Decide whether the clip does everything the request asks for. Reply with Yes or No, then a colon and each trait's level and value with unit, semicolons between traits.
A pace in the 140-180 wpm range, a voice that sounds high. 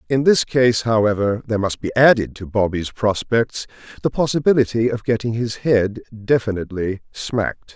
No: average, 145 wpm; low, 115 Hz